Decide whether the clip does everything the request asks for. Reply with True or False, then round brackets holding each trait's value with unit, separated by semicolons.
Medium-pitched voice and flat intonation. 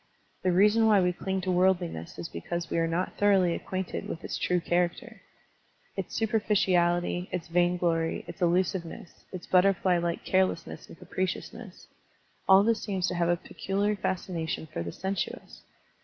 True (180 Hz; 1.9 semitones)